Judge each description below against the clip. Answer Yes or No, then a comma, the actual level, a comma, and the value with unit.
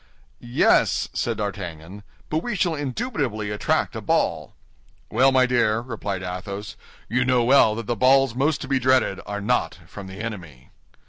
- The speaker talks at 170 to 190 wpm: No, average, 160 wpm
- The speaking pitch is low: Yes, low, 115 Hz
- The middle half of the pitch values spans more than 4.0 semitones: Yes, average, 4.5 semitones